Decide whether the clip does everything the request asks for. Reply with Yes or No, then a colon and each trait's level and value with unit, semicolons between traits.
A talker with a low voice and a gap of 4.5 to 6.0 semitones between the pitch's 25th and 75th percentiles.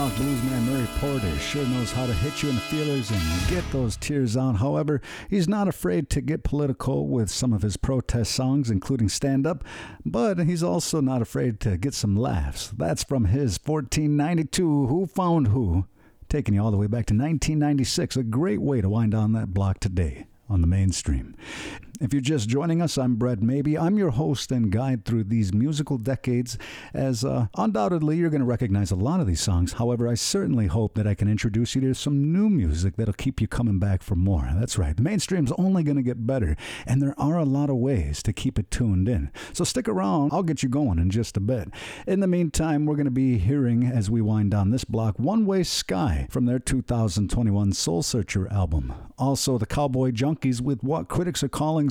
Yes: low, 125 Hz; average, 5.3 semitones